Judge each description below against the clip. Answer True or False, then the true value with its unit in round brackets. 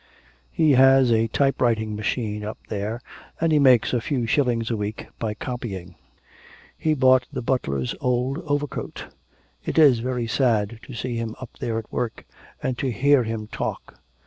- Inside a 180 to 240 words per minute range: False (170 wpm)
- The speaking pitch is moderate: False (120 Hz)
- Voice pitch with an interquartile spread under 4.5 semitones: True (3.1 semitones)